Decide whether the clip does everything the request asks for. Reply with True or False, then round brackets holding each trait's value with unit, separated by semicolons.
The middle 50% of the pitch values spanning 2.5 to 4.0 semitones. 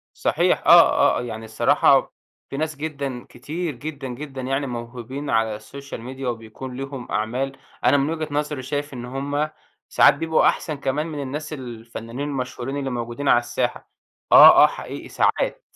True (3.0 semitones)